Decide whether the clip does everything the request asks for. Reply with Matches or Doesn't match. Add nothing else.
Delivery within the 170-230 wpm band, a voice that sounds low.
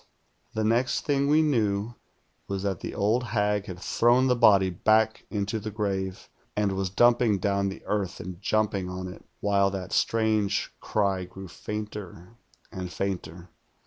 Doesn't match